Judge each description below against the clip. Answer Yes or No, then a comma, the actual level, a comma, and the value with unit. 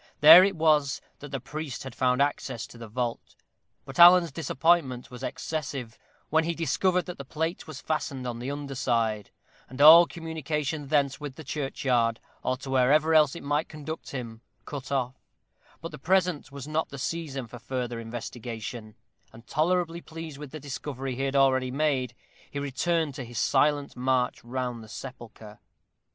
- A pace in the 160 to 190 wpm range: Yes, average, 170 wpm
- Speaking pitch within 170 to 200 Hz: No, medium, 140 Hz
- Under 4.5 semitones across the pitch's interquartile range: Yes, average, 3.8 semitones